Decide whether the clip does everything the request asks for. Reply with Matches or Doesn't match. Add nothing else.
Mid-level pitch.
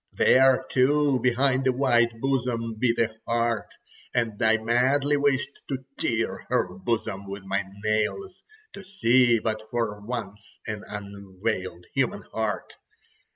Doesn't match